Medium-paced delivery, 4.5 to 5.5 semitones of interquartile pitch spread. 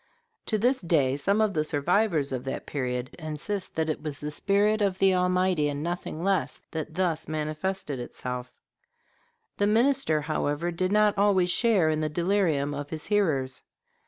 Yes: average, 165 wpm; average, 5.0 semitones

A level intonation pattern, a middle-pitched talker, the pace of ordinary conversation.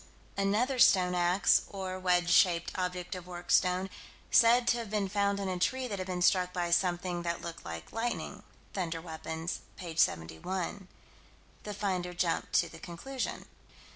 Yes: narrow, 2.3 semitones; medium, 180 Hz; average, 165 wpm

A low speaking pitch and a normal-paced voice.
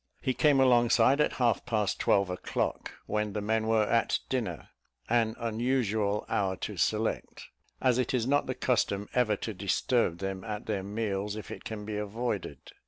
Yes: low, 110 Hz; average, 170 wpm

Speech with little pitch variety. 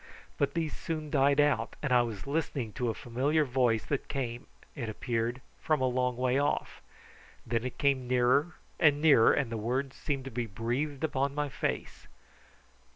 No: average, 3.2 semitones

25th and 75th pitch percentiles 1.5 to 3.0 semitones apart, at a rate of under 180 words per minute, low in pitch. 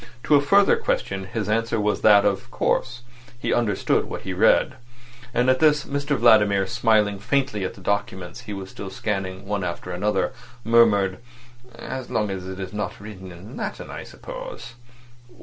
No: average, 3.8 semitones; average, 165 wpm; low, 105 Hz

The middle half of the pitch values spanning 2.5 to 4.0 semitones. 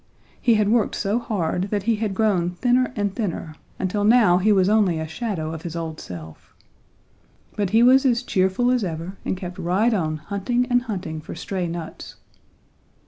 No: average, 4.7 semitones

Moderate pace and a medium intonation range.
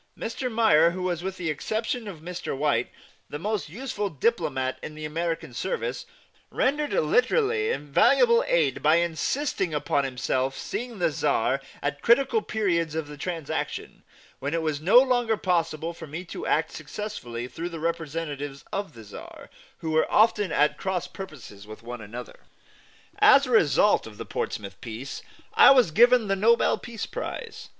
No: average, 160 wpm; wide, 7.5 semitones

